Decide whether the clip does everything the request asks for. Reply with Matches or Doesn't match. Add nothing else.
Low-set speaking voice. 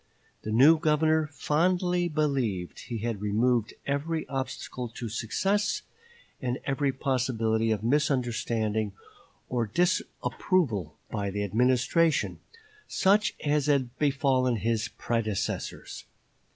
Matches